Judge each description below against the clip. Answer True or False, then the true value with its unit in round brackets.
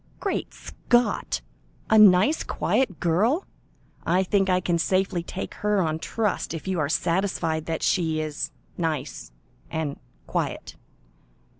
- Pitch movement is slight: False (3.9 semitones)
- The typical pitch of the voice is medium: True (180 Hz)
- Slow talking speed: True (130 wpm)